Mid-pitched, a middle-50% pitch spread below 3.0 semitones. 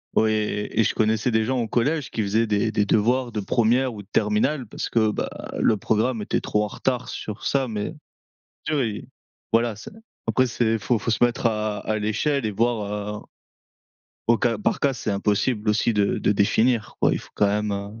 No: low, 110 Hz; narrow, 2.5 semitones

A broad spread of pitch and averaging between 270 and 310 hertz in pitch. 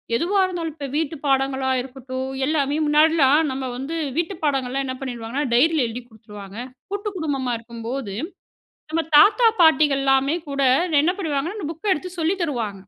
No: average, 3.8 semitones; very high, 275 Hz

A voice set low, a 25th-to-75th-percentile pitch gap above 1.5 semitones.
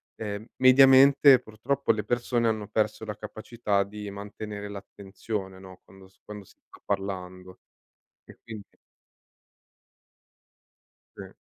Yes: low, 105 Hz; narrow, 2.5 semitones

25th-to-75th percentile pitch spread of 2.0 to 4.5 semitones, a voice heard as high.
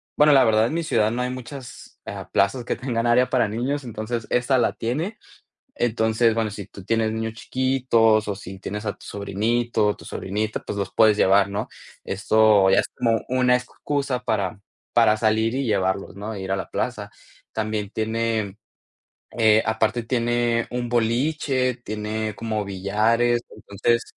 No: narrow, 2.5 semitones; low, 110 Hz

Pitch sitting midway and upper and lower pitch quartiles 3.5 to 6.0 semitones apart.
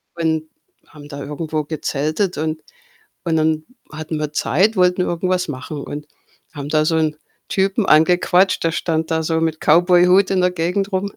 No: medium, 160 Hz; average, 2.7 semitones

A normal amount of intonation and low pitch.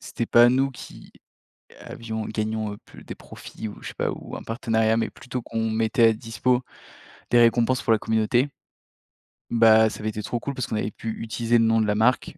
No: narrow, 1.4 semitones; low, 115 Hz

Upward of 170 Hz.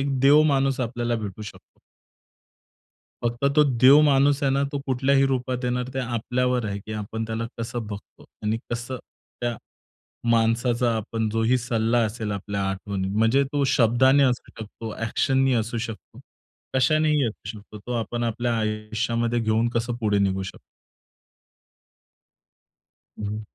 No: low, 120 Hz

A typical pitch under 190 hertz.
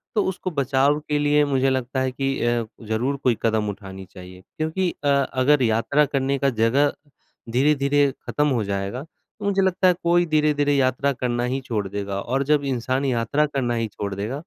Yes: low, 135 Hz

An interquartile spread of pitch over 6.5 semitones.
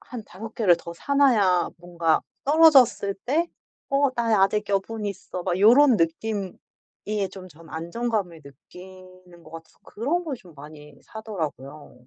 No: wide, 5.4 semitones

